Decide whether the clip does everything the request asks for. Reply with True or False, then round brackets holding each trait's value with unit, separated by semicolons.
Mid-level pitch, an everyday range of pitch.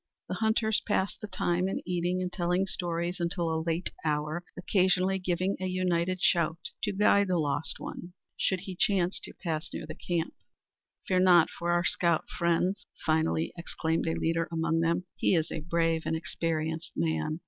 False (175 Hz; 2.1 semitones)